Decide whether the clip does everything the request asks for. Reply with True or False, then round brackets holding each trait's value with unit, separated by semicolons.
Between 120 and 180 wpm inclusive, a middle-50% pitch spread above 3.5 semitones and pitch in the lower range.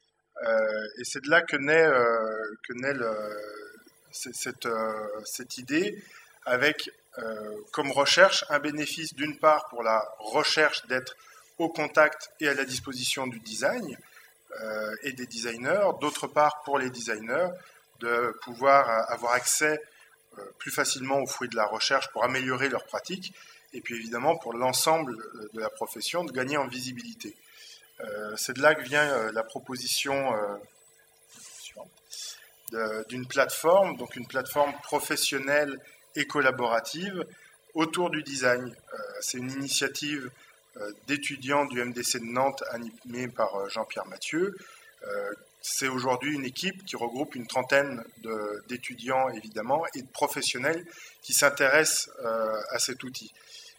True (145 wpm; 4.1 semitones; 130 Hz)